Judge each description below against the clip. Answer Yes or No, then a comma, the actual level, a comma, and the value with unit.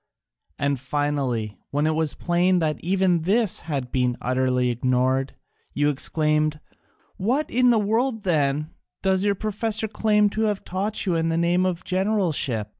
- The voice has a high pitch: No, medium, 165 Hz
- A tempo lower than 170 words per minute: Yes, average, 155 wpm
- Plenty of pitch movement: Yes, wide, 6.4 semitones